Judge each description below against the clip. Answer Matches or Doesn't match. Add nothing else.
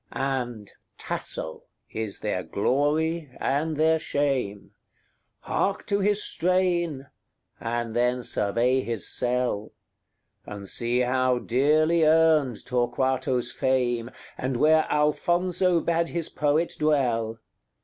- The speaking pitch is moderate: Doesn't match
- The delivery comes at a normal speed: Doesn't match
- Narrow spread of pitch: Doesn't match